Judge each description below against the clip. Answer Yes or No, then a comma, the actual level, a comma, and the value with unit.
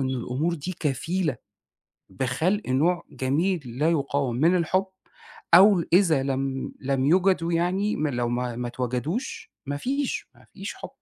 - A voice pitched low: No, medium, 150 Hz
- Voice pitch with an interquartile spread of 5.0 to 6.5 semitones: Yes, wide, 5.5 semitones